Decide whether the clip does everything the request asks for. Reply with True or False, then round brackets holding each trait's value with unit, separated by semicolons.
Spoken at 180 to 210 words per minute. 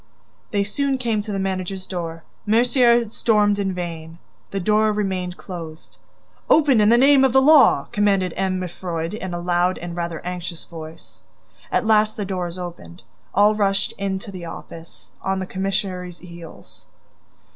False (165 wpm)